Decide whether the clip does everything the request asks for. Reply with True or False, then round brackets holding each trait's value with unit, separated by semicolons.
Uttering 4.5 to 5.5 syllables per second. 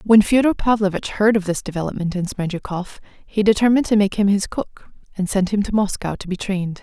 False (5.8 syllables/s)